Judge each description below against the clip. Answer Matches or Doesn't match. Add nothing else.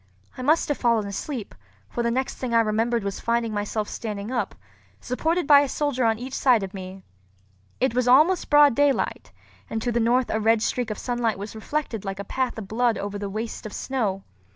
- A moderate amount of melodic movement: Matches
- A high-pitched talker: Matches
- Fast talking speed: Matches